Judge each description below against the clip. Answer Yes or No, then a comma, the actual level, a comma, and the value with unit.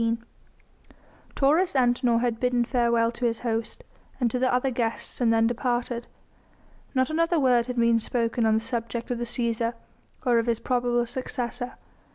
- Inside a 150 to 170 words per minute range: Yes, average, 165 wpm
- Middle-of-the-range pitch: No, high, 240 Hz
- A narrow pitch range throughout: Yes, narrow, 1.3 semitones